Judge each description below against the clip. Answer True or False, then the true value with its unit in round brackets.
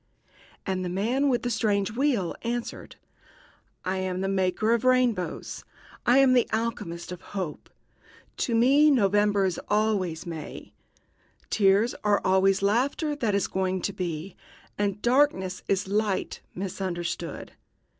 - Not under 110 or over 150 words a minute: True (135 wpm)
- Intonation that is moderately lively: True (4.0 semitones)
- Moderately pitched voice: False (200 Hz)